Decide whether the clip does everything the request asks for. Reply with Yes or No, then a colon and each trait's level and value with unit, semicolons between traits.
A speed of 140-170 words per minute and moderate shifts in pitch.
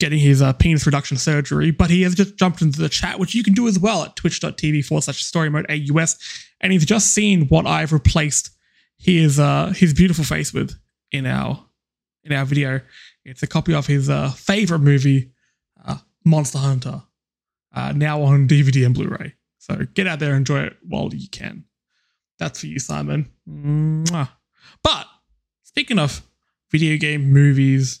No: average, 180 wpm; average, 3.4 semitones